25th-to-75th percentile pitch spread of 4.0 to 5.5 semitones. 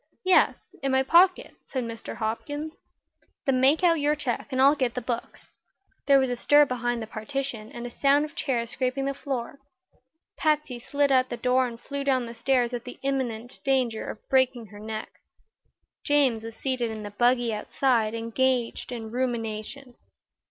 No: average, 2.9 semitones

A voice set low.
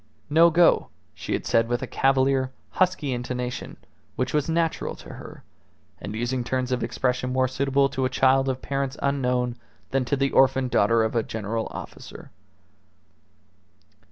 Yes: low, 130 Hz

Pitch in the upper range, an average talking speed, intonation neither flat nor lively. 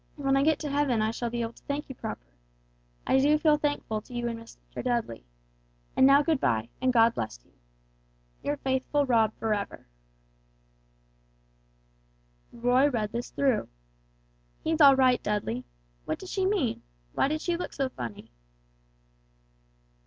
Yes: very high, 255 Hz; average, 155 wpm; average, 4.2 semitones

